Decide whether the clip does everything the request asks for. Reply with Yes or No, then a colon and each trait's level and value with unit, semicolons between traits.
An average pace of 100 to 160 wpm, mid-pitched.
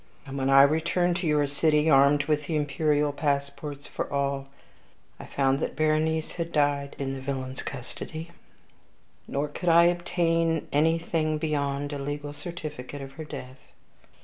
Yes: average, 150 wpm; medium, 145 Hz